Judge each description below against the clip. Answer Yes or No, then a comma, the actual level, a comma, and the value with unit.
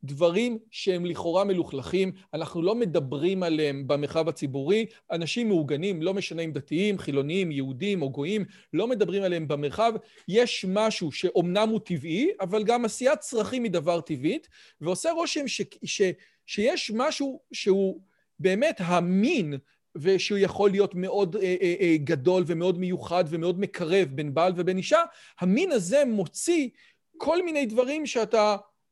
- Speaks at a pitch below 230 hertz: Yes, high, 190 Hz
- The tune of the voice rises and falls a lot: No, average, 4.3 semitones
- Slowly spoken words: No, average, 145 wpm